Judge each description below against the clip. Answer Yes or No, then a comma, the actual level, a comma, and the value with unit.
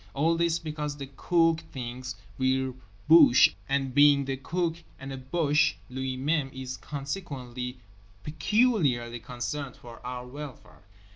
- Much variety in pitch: No, average, 3.4 semitones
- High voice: No, medium, 140 Hz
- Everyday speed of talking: No, slow, 130 wpm